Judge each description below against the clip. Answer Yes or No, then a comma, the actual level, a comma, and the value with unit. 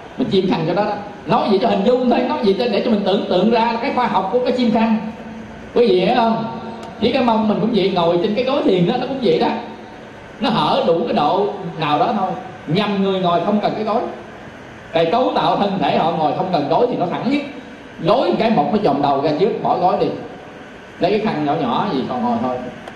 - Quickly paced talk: Yes, fast, 255 wpm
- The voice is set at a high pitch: Yes, high, 225 Hz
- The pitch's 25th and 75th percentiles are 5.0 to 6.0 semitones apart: No, average, 4.2 semitones